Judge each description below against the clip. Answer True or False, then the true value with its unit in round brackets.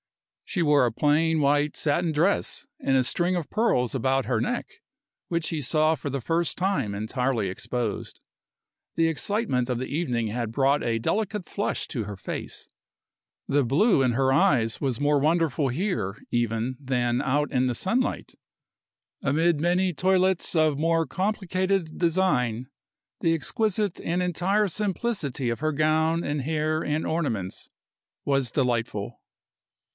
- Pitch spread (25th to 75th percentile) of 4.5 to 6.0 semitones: True (5.5 semitones)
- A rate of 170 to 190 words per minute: False (145 wpm)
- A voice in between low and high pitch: True (150 Hz)